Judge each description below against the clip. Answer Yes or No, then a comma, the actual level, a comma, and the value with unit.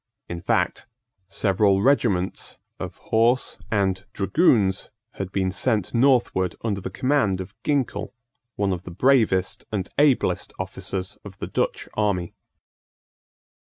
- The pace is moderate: No, slow, 120 wpm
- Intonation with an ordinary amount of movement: Yes, average, 4.3 semitones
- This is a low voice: Yes, low, 100 Hz